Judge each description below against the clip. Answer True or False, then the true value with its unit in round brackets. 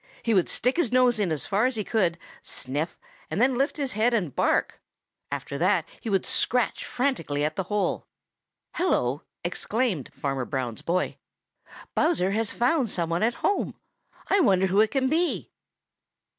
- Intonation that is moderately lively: False (6.9 semitones)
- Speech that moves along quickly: False (165 wpm)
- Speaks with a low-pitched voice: False (210 Hz)